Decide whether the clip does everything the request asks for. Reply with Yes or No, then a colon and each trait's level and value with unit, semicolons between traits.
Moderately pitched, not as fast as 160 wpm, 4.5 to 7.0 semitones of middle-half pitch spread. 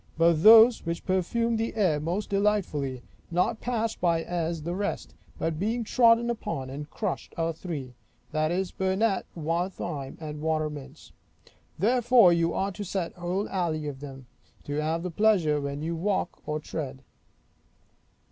Yes: medium, 170 Hz; average, 150 wpm; average, 5.0 semitones